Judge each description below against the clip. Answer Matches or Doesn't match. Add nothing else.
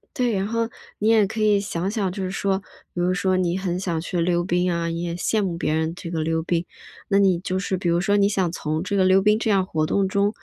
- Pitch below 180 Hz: Doesn't match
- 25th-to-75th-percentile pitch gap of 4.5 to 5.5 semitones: Doesn't match